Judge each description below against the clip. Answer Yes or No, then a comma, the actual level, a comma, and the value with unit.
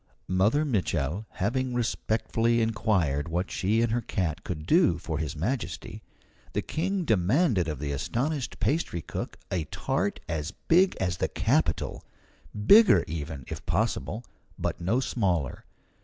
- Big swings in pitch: Yes, wide, 6.9 semitones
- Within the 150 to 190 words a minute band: No, average, 140 wpm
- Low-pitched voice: Yes, low, 100 Hz